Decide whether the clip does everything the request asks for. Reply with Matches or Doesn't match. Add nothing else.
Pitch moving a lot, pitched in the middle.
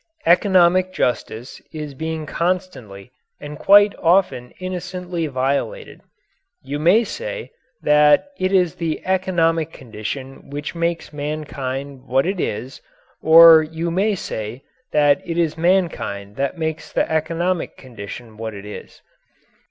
Doesn't match